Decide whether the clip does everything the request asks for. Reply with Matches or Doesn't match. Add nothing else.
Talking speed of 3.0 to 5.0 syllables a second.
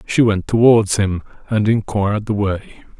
Matches